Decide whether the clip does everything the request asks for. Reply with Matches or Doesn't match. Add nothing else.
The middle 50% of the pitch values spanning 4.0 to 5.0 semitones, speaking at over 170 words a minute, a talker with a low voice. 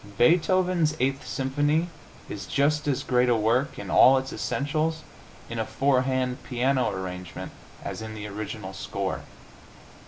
Doesn't match